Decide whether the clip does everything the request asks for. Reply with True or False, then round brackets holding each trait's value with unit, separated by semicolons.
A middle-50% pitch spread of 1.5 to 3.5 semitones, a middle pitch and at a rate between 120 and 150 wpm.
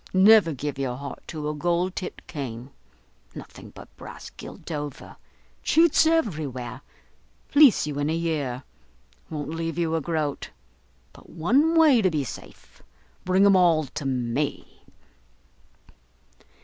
False (4.7 semitones; 160 Hz; 135 wpm)